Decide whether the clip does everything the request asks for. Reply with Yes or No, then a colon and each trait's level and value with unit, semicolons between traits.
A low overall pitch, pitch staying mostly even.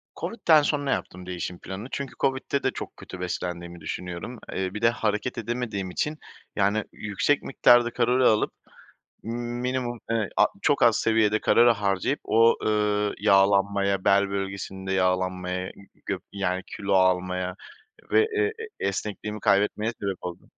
No: low, 105 Hz; average, 4.1 semitones